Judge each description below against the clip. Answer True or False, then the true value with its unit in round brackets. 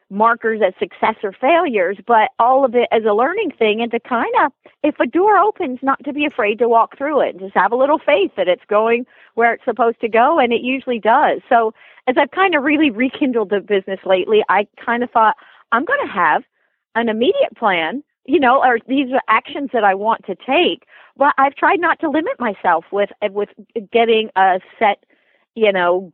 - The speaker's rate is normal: False (215 wpm)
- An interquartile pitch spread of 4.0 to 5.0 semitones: True (4.7 semitones)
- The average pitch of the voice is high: True (235 Hz)